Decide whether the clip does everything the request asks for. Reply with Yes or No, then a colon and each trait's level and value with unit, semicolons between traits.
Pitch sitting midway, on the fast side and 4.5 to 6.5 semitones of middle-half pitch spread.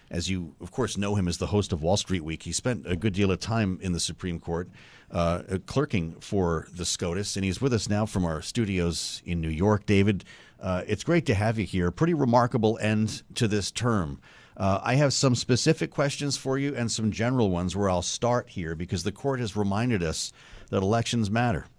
No: low, 100 Hz; fast, 220 wpm; average, 4.8 semitones